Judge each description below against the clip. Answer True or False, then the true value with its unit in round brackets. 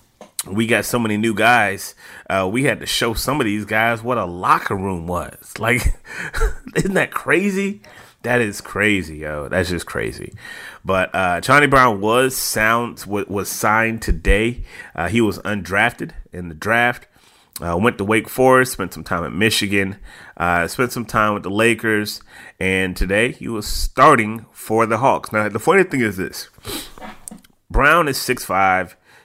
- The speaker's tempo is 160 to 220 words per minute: True (165 wpm)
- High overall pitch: False (105 Hz)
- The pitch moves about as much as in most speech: True (3.7 semitones)